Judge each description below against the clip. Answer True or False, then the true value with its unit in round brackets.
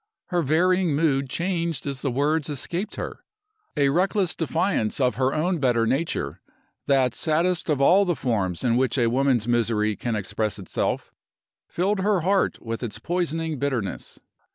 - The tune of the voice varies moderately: False (6.1 semitones)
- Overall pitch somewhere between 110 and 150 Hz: True (140 Hz)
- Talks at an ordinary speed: True (155 wpm)